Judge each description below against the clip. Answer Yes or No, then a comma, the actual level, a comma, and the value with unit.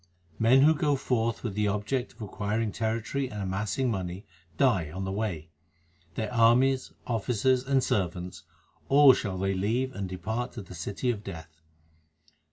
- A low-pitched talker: Yes, low, 110 Hz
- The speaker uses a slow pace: No, average, 160 wpm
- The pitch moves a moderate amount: Yes, average, 4.7 semitones